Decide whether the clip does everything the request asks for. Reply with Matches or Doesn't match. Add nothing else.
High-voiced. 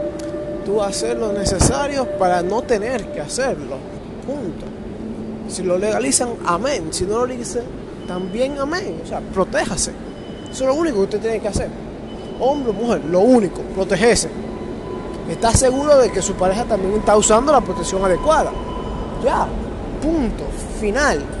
Matches